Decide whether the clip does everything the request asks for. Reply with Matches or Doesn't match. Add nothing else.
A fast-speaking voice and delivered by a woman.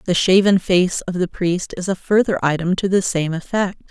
Matches